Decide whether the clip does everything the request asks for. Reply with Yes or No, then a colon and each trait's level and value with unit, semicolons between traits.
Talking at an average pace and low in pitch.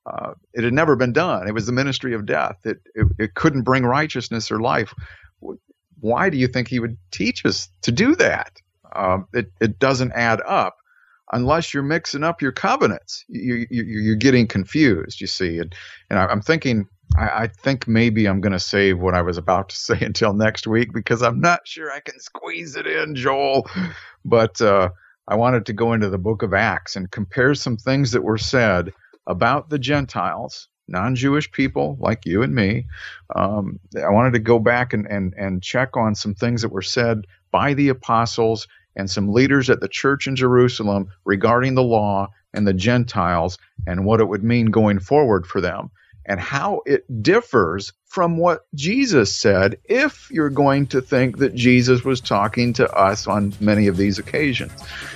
Yes: average, 190 wpm; low, 115 Hz